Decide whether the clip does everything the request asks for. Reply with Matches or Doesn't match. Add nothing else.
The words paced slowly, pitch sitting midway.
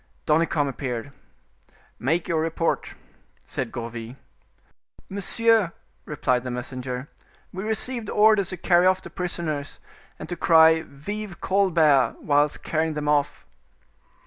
Matches